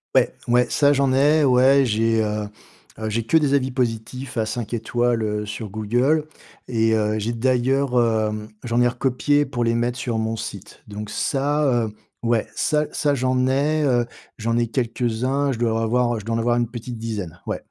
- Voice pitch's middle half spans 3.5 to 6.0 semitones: No, average, 2.9 semitones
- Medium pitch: No, low, 120 Hz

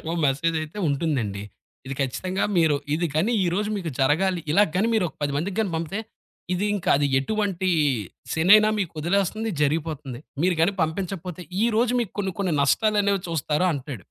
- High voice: No, medium, 175 Hz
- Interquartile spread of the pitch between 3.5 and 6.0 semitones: Yes, average, 4.9 semitones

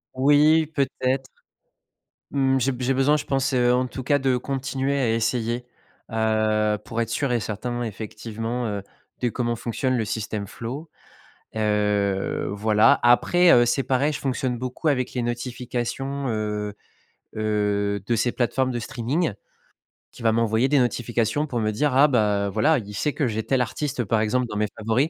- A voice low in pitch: Yes, low, 120 Hz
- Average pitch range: Yes, average, 3.4 semitones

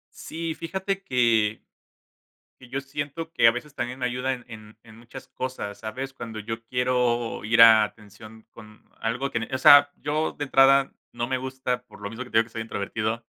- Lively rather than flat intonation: No, average, 3.1 semitones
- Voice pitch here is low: Yes, low, 125 Hz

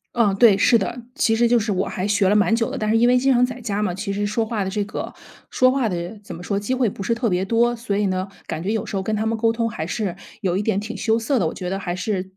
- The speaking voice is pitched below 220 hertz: Yes, high, 210 Hz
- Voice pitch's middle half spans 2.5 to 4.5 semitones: Yes, average, 3.1 semitones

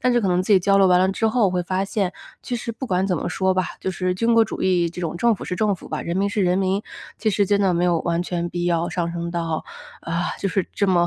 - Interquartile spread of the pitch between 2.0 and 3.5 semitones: Yes, narrow, 2.4 semitones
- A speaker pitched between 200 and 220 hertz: No, medium, 185 Hz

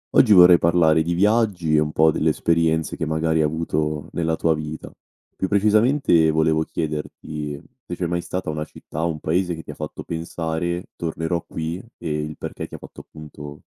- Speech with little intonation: Yes, narrow, 2.0 semitones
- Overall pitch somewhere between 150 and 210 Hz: No, very low, 80 Hz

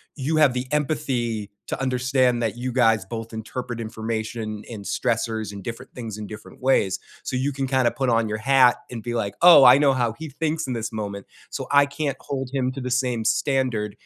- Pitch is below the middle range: Yes, low, 125 Hz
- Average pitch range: Yes, average, 3.2 semitones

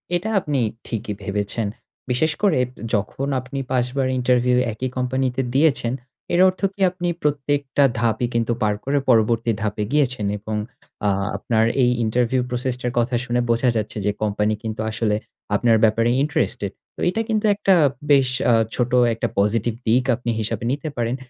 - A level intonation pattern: No, average, 3.4 semitones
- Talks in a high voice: No, low, 120 Hz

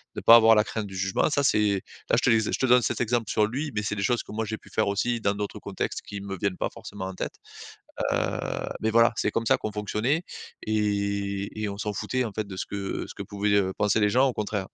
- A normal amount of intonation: No, narrow, 2.1 semitones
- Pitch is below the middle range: Yes, low, 105 Hz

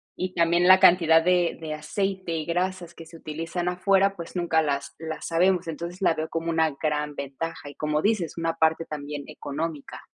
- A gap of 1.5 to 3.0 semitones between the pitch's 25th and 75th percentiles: Yes, narrow, 2.5 semitones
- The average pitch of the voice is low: No, medium, 165 Hz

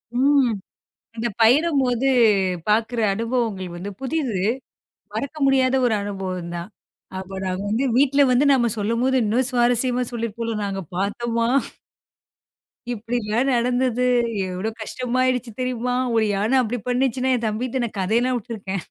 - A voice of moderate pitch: No, high, 235 Hz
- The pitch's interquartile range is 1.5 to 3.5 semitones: Yes, average, 3.2 semitones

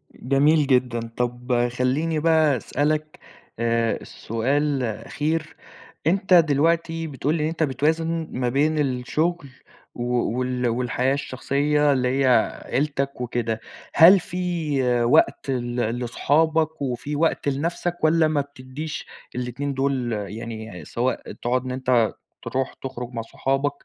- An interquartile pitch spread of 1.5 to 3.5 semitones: No, average, 4.0 semitones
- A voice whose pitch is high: No, low, 135 Hz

